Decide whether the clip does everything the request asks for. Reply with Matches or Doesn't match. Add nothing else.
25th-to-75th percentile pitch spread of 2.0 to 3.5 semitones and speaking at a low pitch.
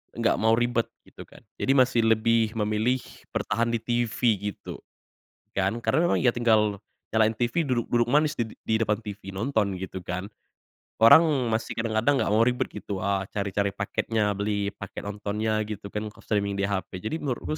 Matches